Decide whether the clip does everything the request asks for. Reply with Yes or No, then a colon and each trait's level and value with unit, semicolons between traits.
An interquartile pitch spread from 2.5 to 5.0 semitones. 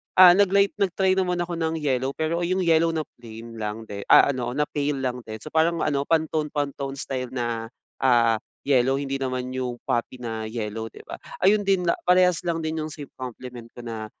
No: wide, 5.5 semitones